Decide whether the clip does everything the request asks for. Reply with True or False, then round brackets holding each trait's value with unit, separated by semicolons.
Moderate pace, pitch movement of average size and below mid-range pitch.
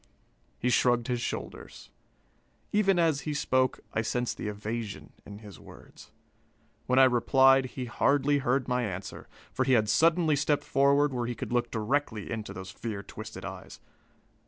True (160 wpm; 3.7 semitones; 125 Hz)